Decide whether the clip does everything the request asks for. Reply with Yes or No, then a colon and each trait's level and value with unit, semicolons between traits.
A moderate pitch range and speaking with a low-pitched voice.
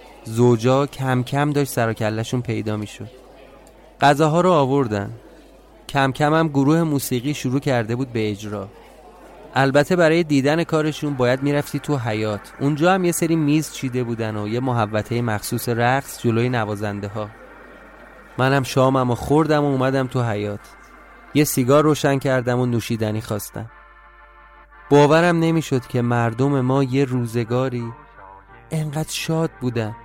Yes: average, 3.9 semitones; low, 130 Hz